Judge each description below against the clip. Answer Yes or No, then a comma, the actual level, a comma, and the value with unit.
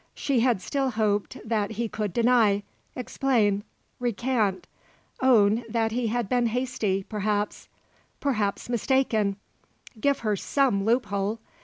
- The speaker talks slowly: Yes, slow, 120 wpm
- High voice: Yes, high, 225 Hz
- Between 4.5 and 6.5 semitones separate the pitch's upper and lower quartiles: No, average, 3.3 semitones